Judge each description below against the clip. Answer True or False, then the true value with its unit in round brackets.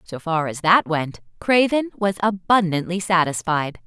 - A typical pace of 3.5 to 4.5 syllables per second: True (4.3 syllables/s)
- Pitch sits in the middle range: True (180 Hz)